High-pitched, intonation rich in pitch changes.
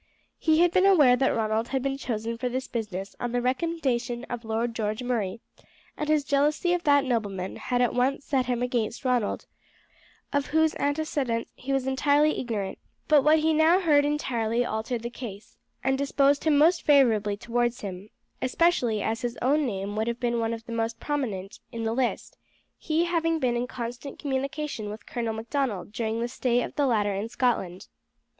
No: high, 245 Hz; average, 4.1 semitones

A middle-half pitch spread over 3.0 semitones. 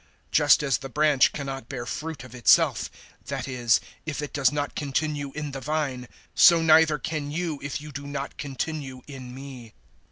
No: narrow, 2.5 semitones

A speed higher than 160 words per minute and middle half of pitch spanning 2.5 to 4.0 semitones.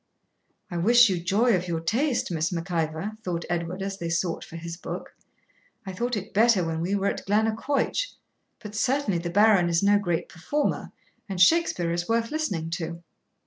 No: average, 185 wpm; average, 4.5 semitones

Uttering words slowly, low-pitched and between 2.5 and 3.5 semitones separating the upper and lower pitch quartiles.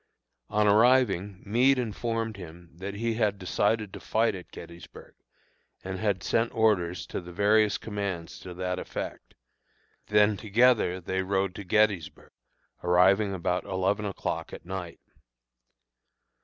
Yes: slow, 130 wpm; low, 100 Hz; average, 2.9 semitones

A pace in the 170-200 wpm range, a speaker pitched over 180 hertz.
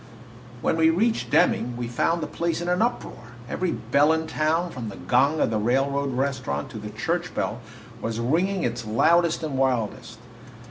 No: average, 180 wpm; medium, 140 Hz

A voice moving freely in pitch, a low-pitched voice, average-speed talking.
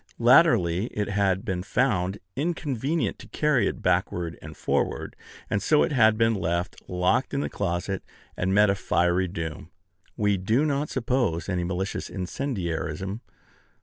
Yes: wide, 5.7 semitones; low, 100 Hz; average, 150 wpm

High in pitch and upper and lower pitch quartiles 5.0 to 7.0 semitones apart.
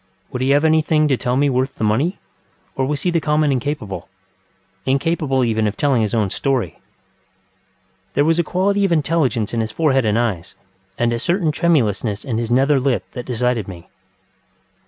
No: low, 130 Hz; wide, 5.5 semitones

